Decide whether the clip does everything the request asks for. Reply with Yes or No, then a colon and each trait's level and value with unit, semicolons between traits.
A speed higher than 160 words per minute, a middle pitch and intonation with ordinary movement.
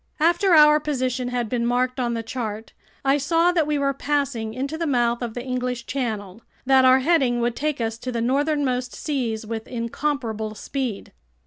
No: average, 185 wpm; very high, 255 Hz; average, 3.5 semitones